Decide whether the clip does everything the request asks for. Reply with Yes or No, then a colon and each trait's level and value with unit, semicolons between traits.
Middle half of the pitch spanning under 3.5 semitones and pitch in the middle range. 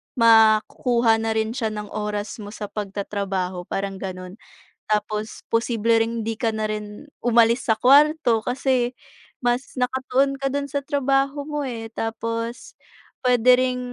No: average, 3.1 semitones; high, 230 Hz